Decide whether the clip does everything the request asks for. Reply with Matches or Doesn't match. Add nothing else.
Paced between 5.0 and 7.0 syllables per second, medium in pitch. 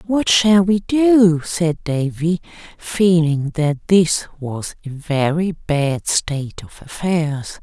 Doesn't match